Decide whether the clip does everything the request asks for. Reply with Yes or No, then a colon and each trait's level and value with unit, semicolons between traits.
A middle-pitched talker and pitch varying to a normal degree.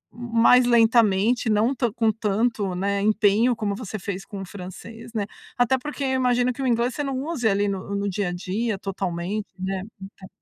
No: high, 215 Hz; average, 3.5 semitones